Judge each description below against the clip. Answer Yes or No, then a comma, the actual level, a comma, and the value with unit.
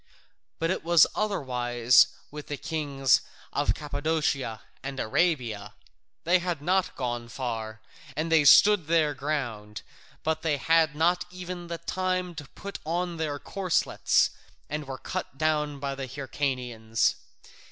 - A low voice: No, medium, 150 Hz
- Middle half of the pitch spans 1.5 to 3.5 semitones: No, average, 4.3 semitones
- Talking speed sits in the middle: No, slow, 130 wpm